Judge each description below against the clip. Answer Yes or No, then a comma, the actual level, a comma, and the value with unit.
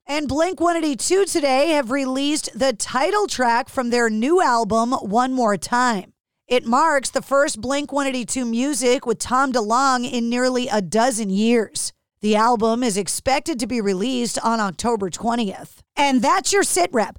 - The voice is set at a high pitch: Yes, very high, 250 Hz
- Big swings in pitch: No, average, 3.4 semitones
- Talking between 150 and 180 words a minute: Yes, average, 155 wpm